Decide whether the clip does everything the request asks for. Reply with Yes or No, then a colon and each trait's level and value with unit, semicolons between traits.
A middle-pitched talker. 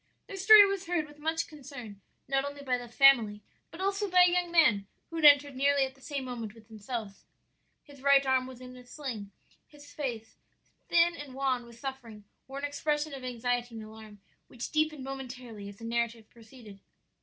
No: very high, 265 Hz